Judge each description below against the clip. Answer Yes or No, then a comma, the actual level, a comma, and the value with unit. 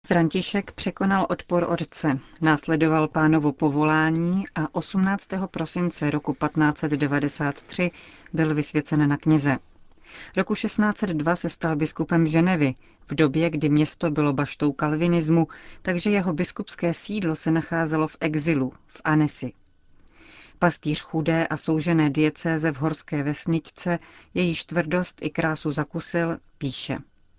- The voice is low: No, medium, 160 Hz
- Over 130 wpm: No, slow, 115 wpm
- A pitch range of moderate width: No, narrow, 2.2 semitones